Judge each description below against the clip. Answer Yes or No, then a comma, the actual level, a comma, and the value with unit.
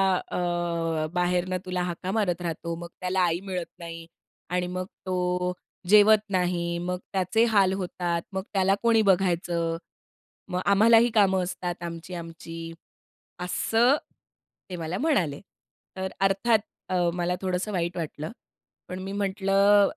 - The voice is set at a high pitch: No, medium, 180 Hz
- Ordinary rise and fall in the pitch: No, narrow, 2.0 semitones